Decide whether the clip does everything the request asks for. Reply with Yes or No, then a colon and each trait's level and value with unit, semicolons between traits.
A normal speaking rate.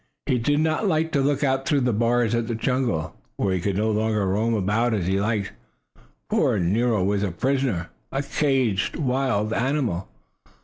Yes: average, 180 wpm